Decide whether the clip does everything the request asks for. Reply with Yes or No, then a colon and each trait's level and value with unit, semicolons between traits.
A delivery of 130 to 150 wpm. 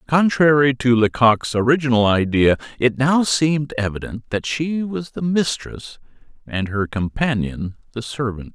Yes: slow, 135 wpm